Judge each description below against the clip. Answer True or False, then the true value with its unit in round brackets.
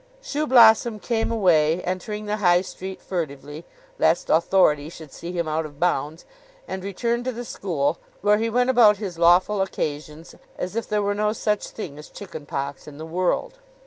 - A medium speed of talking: True (175 wpm)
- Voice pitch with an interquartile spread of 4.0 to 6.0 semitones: True (5.1 semitones)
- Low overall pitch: False (185 Hz)